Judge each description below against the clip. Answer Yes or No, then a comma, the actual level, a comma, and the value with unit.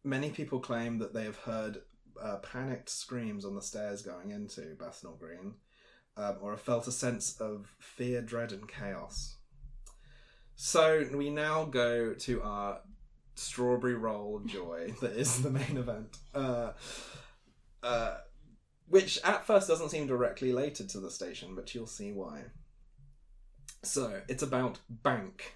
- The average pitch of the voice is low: Yes, low, 125 Hz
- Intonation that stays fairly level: No, average, 3.7 semitones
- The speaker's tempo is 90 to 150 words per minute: Yes, average, 145 wpm